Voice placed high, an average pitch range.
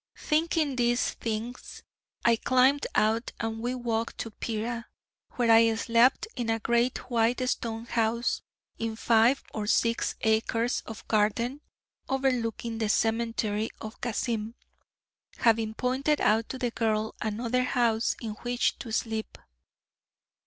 No: high, 230 Hz; narrow, 1.7 semitones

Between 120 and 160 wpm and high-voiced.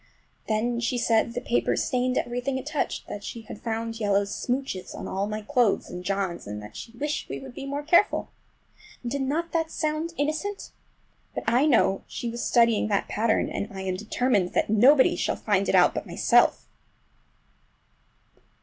No: average, 175 wpm; high, 235 Hz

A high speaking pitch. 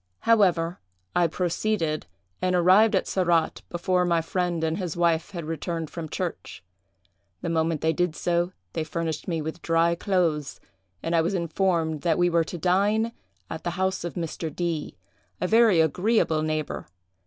No: medium, 170 Hz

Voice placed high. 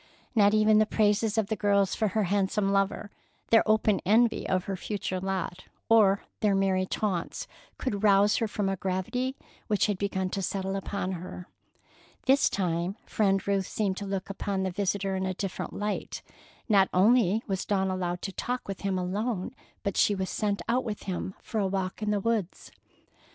Yes: high, 200 Hz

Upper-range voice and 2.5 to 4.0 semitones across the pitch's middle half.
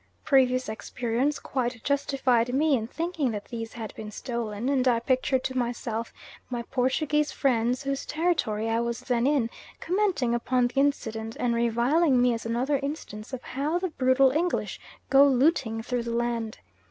Yes: very high, 250 Hz; average, 3.0 semitones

